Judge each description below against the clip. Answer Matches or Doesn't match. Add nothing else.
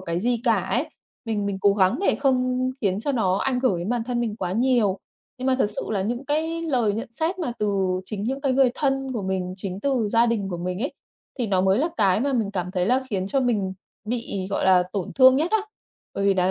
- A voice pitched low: Doesn't match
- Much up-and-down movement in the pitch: Doesn't match